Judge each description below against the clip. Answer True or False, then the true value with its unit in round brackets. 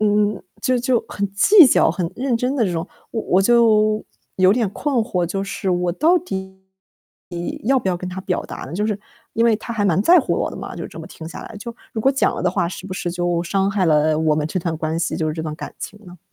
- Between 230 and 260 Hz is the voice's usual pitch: False (195 Hz)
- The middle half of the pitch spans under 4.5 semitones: False (4.8 semitones)